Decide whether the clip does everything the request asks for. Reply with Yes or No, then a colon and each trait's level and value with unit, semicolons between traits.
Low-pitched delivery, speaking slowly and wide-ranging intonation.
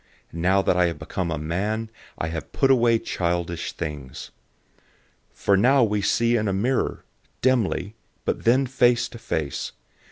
No: low, 100 Hz; average, 160 wpm; wide, 5.7 semitones